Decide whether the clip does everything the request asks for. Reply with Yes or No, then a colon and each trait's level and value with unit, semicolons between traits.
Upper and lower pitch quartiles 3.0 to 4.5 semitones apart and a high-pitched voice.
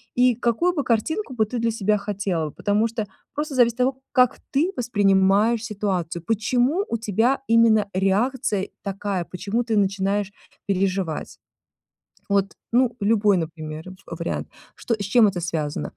Yes: average, 3.7 semitones; high, 210 Hz